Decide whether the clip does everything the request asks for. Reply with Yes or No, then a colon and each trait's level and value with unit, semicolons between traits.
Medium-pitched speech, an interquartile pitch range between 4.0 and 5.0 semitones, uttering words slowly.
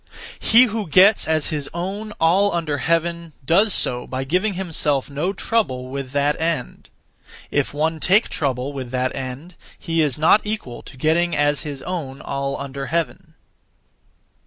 No: medium, 155 Hz; average, 4.5 semitones; average, 160 wpm